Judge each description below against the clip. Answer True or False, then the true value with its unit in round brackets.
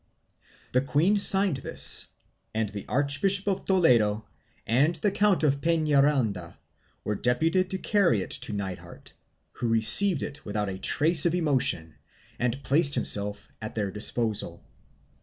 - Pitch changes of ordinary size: False (7.9 semitones)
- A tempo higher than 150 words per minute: False (140 wpm)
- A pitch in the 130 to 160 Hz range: True (135 Hz)